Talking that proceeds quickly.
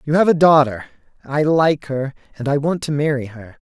No: average, 180 wpm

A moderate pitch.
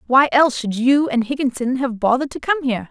No: very high, 260 Hz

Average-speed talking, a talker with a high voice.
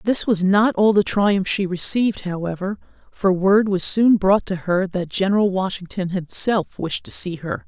Yes: average, 190 wpm; high, 195 Hz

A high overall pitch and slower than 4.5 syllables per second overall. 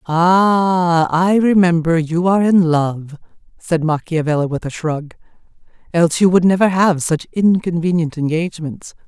No: medium, 170 Hz; 4.3 syllables/s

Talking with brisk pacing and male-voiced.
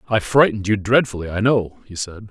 Yes: fast, 210 wpm; male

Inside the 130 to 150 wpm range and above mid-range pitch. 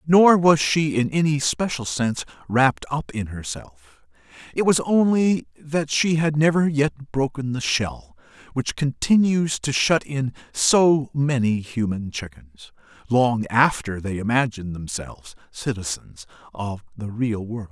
No: average, 140 wpm; low, 130 Hz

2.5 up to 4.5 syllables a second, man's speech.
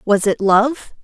No: 3.5 syllables/s; female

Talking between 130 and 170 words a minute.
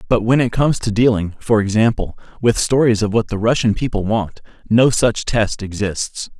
No: average, 190 wpm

